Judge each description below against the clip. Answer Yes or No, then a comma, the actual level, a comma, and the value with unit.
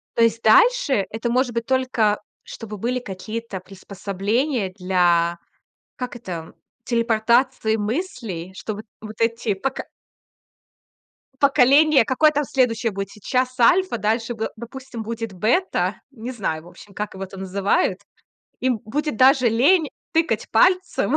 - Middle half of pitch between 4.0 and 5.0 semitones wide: Yes, average, 4.3 semitones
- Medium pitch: No, high, 230 Hz